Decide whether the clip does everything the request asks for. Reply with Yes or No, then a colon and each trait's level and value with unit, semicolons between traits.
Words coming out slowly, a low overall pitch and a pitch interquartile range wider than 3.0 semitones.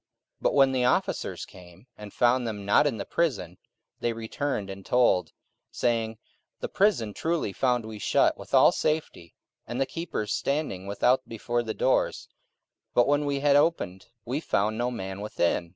No: average, 175 wpm; low, 120 Hz; average, 5.2 semitones